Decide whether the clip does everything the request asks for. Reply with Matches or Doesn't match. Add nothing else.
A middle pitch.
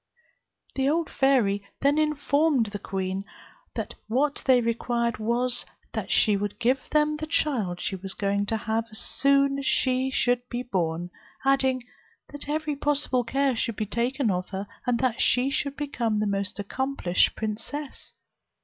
Doesn't match